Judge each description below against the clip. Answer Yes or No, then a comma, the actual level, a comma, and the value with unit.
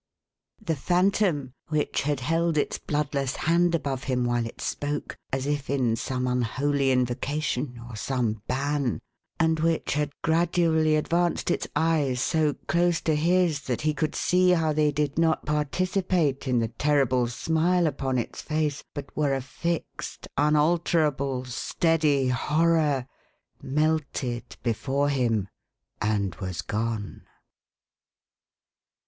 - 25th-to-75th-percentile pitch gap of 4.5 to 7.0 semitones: No, average, 4.0 semitones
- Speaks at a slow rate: Yes, slow, 130 wpm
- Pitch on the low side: No, medium, 145 Hz